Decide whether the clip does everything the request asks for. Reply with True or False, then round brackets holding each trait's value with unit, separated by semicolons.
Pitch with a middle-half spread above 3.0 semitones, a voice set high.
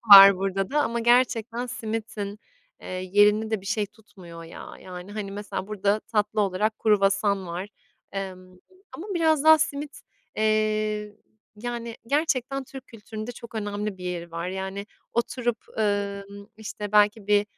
False (2.7 semitones; 210 Hz)